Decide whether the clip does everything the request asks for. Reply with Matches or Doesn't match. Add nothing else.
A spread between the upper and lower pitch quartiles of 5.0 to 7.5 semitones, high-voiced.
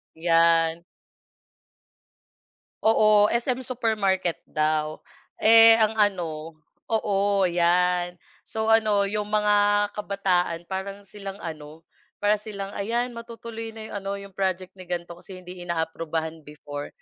Doesn't match